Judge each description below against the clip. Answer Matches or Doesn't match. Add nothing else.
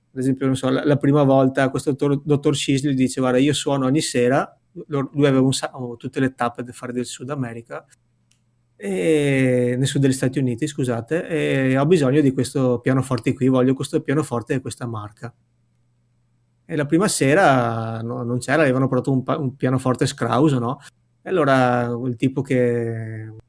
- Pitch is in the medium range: Doesn't match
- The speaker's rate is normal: Doesn't match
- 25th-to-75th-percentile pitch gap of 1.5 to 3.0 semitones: Matches